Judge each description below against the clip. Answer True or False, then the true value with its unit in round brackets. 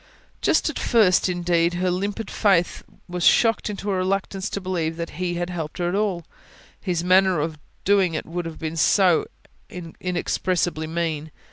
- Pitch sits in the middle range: True (180 Hz)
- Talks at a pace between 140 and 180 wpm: True (165 wpm)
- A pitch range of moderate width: False (2.2 semitones)